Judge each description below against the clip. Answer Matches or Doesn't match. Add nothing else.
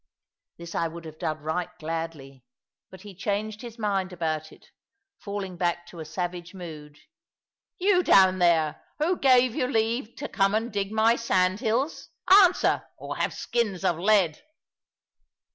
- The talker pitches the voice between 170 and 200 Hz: Matches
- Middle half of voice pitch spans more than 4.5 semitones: Matches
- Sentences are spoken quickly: Doesn't match